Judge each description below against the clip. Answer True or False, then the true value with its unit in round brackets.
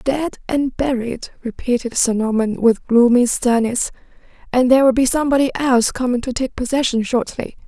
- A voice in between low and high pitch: False (250 Hz)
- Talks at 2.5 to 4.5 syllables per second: False (5.3 syllables/s)